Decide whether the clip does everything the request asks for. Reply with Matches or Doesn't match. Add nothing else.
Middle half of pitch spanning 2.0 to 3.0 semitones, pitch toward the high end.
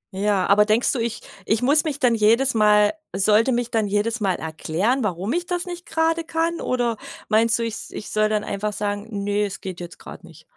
Doesn't match